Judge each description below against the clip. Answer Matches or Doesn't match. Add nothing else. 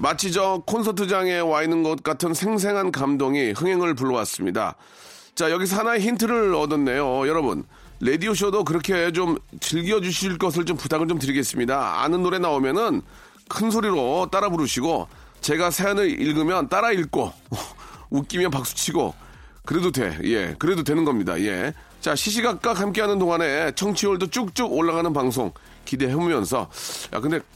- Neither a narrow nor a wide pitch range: Matches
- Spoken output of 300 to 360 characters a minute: Matches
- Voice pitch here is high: Doesn't match